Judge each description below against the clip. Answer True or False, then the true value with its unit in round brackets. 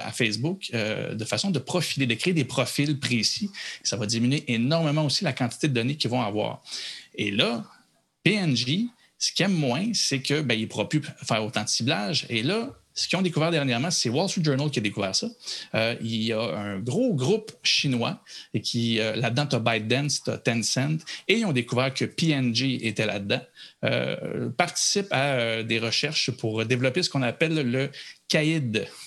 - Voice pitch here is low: True (130 Hz)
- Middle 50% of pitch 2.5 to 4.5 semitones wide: False (5.2 semitones)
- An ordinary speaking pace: True (195 wpm)